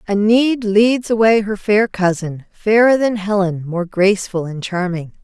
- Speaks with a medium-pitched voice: No, high, 200 Hz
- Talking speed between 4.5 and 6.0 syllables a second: Yes, 4.6 syllables/s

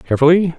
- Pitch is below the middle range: No, medium, 160 Hz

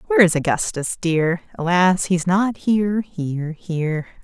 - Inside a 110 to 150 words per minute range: Yes, average, 140 wpm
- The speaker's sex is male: No, female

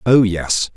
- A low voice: Yes, low, 105 Hz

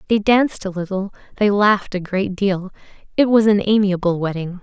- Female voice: Yes, female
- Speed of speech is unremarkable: Yes, average, 180 wpm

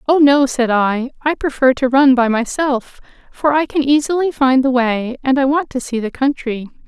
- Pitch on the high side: Yes, very high, 265 Hz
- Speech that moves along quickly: Yes, fast, 210 wpm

